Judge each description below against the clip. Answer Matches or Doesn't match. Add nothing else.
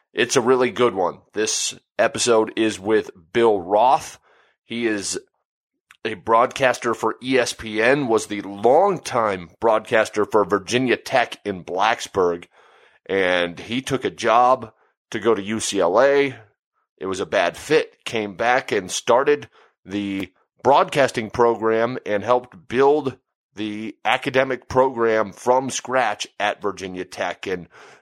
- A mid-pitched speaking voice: Doesn't match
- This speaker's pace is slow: Matches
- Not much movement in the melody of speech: Doesn't match